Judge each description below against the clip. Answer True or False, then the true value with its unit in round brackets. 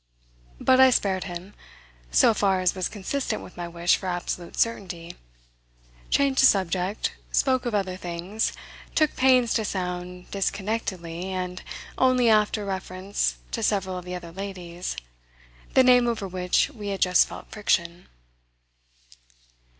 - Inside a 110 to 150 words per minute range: True (140 wpm)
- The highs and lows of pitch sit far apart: False (3.5 semitones)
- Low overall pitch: False (190 Hz)